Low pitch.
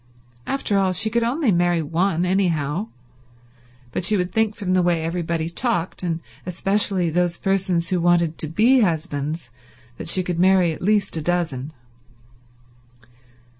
No: medium, 175 Hz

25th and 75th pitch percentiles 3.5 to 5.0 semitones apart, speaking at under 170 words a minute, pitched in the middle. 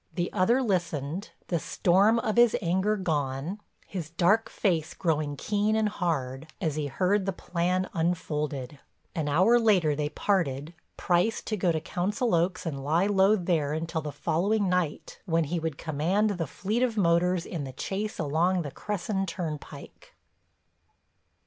Yes: average, 4.3 semitones; average, 155 wpm; medium, 175 Hz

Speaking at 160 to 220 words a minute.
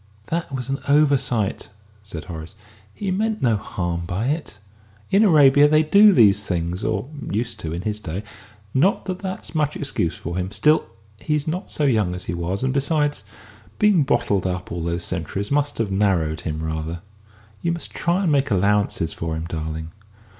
Yes: average, 180 wpm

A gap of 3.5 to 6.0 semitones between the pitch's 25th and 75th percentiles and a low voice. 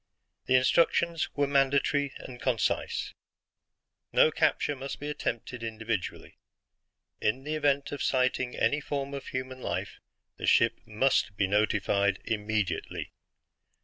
Yes: average, 4.4 semitones; low, 130 Hz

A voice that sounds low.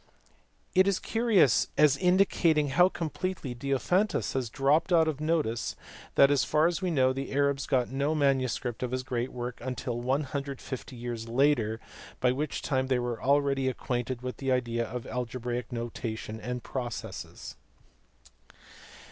Yes: low, 130 Hz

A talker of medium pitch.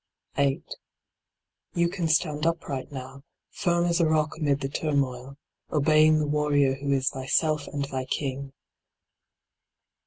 Yes: medium, 145 Hz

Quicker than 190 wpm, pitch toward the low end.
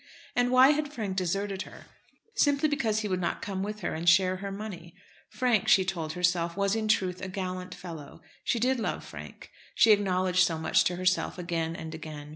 No: average, 200 wpm; medium, 185 Hz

